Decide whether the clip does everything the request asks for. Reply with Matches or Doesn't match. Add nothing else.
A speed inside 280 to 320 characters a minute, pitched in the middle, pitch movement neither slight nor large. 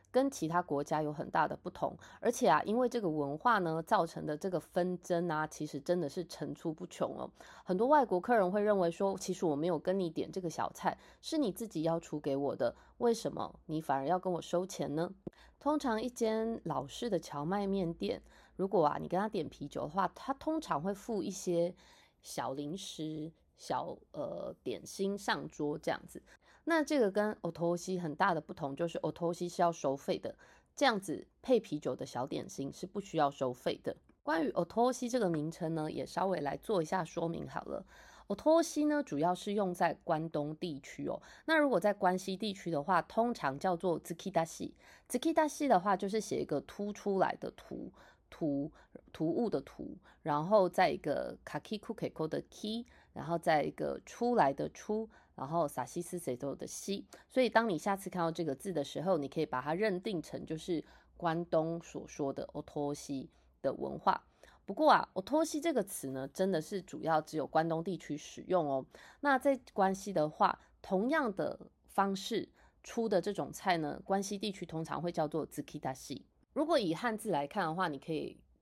Matches